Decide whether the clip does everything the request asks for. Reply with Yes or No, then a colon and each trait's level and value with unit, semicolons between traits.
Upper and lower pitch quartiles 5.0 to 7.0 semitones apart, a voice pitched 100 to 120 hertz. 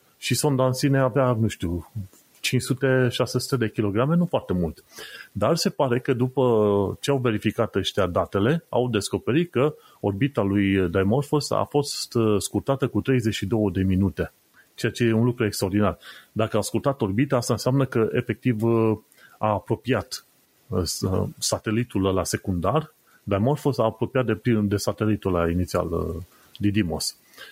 No: average, 4.2 semitones; low, 110 Hz